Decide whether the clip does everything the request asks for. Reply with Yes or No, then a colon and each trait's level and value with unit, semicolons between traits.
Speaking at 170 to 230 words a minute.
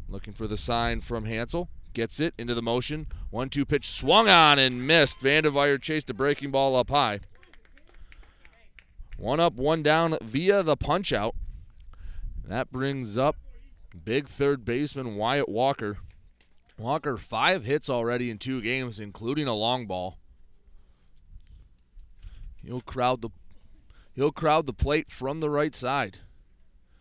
No: average, 140 wpm